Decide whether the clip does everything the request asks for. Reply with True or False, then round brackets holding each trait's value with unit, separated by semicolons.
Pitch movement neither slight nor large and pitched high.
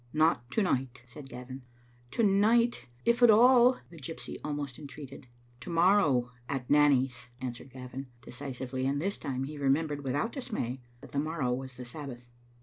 False (4.7 semitones; 140 Hz)